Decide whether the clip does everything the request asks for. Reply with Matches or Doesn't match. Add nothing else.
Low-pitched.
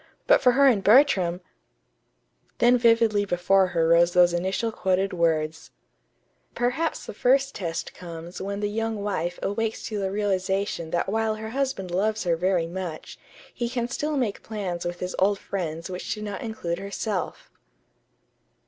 Doesn't match